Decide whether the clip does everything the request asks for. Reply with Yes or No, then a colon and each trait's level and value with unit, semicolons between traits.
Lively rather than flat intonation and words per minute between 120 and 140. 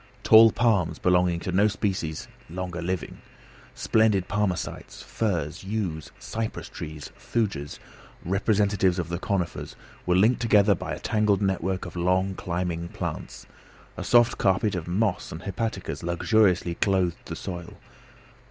No: average, 3.2 semitones; slow, 135 wpm